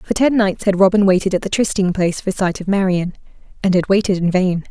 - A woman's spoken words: Yes, female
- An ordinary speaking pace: No, fast, 240 wpm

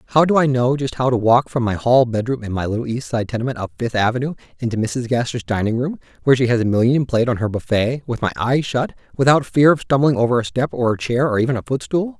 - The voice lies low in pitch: Yes, low, 125 Hz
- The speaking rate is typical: No, fast, 265 wpm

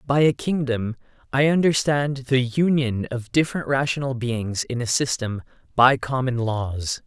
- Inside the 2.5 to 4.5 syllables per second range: Yes, 4.4 syllables/s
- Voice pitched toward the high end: No, low, 130 Hz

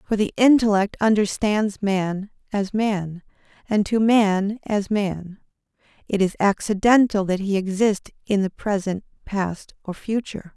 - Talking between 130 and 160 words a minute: Yes, slow, 135 wpm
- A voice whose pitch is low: No, high, 205 Hz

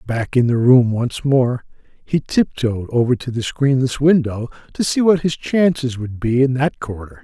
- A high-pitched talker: No, low, 130 Hz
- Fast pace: No, average, 190 wpm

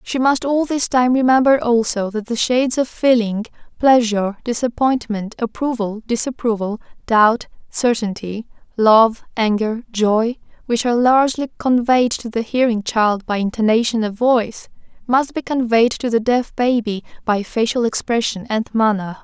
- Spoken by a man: No, female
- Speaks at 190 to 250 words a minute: No, average, 140 wpm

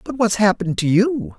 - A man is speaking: Yes, male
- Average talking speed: No, fast, 215 wpm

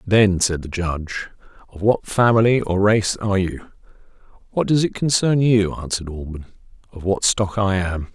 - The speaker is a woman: No, male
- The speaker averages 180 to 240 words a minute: No, average, 160 wpm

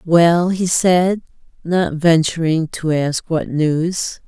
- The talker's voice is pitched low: No, medium, 165 Hz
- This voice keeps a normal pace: No, slow, 125 wpm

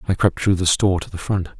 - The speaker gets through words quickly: Yes, fast, 300 wpm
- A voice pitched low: Yes, very low, 90 Hz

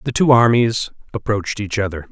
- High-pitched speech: No, low, 110 Hz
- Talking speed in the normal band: Yes, average, 170 wpm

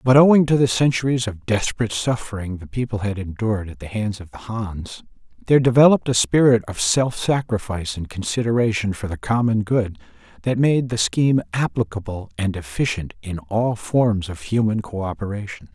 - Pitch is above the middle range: No, low, 110 Hz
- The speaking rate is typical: Yes, average, 170 wpm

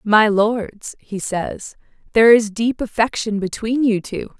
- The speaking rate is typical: Yes, average, 150 wpm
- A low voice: No, high, 220 Hz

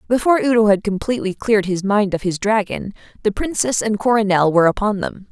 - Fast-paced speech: No, average, 190 wpm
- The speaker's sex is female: Yes, female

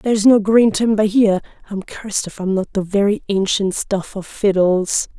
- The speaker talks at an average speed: Yes, average, 185 wpm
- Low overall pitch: No, high, 200 Hz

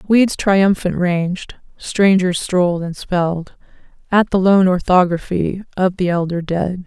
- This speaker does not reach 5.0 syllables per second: Yes, 4.1 syllables/s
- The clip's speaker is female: Yes, female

